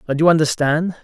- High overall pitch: No, medium, 155 Hz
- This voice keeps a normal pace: Yes, average, 175 wpm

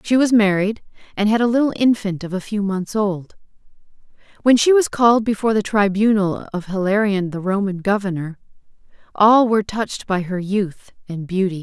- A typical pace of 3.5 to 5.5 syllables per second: Yes, 5.3 syllables/s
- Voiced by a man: No, female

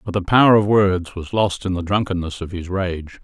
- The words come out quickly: Yes, fast, 240 wpm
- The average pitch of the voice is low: Yes, very low, 95 Hz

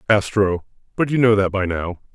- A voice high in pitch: No, low, 100 Hz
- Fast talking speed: No, average, 195 wpm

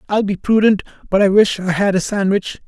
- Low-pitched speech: No, high, 200 Hz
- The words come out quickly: Yes, fast, 225 wpm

